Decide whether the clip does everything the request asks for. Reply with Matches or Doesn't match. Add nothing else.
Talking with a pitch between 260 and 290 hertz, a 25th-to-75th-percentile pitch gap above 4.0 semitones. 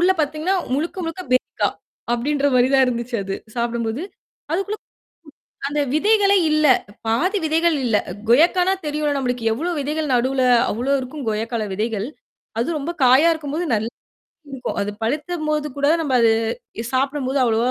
Matches